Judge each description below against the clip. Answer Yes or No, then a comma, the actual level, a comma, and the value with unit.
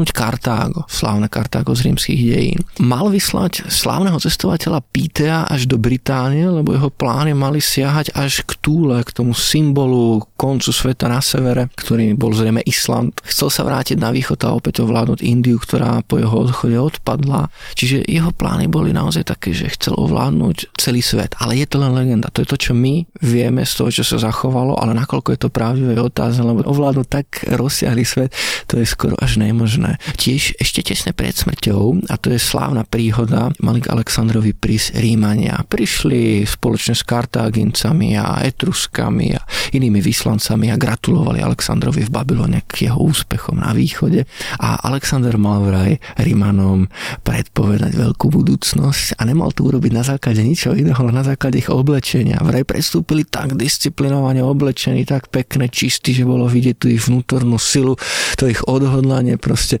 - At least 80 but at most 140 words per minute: No, average, 160 wpm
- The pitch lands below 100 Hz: No, low, 130 Hz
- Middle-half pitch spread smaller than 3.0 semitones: No, average, 3.3 semitones